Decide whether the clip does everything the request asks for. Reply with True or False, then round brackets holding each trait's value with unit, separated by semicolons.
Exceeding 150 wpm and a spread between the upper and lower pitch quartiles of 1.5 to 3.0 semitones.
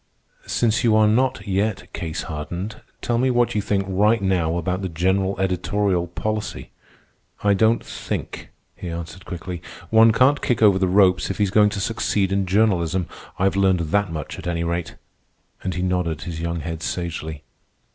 False (175 wpm; 3.4 semitones)